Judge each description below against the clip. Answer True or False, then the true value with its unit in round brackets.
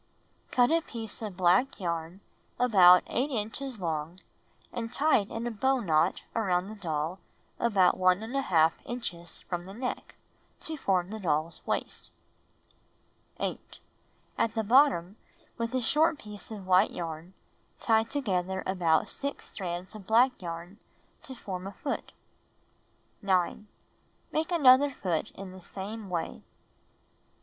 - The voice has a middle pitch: False (200 Hz)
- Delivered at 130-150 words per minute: True (140 wpm)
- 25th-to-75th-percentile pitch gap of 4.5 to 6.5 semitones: True (5.2 semitones)